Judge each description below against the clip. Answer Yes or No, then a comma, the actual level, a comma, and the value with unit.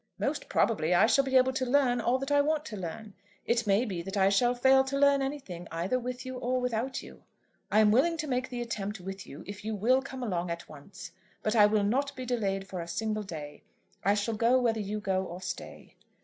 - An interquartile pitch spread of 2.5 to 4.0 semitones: No, average, 4.9 semitones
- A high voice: Yes, high, 225 Hz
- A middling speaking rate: No, fast, 235 wpm